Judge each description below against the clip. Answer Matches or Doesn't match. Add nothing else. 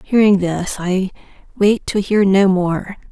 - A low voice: Doesn't match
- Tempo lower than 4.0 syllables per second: Matches